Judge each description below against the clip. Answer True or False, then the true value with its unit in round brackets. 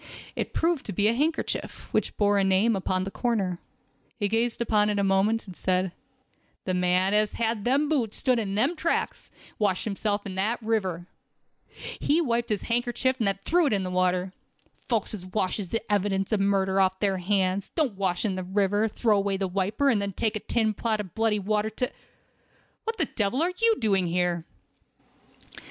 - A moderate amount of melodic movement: True (3.3 semitones)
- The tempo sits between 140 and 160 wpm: False (200 wpm)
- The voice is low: False (205 Hz)